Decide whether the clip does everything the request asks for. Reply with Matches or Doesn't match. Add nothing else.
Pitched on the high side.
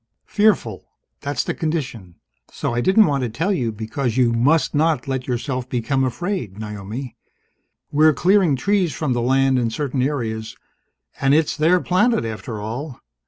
Doesn't match